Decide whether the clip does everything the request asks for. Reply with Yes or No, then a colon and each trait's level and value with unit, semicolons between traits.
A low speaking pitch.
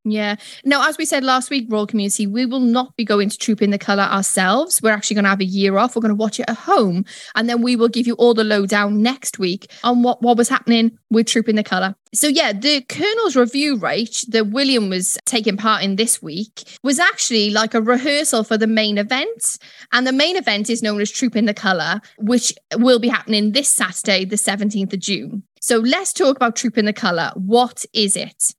No: high, 225 Hz